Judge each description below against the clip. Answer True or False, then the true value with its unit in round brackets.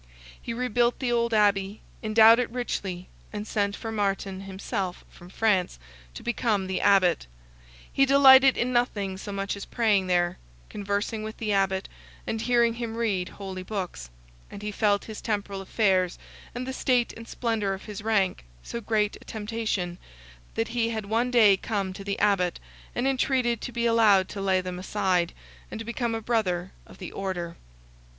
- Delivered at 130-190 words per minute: True (170 wpm)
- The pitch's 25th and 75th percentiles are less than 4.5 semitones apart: True (3.1 semitones)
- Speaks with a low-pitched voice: False (210 Hz)